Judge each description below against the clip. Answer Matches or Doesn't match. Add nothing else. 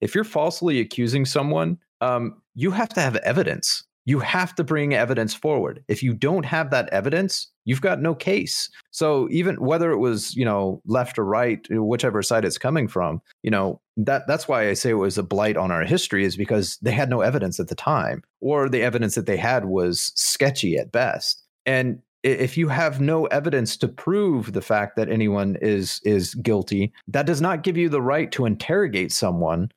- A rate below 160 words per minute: Doesn't match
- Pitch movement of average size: Doesn't match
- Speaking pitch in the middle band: Doesn't match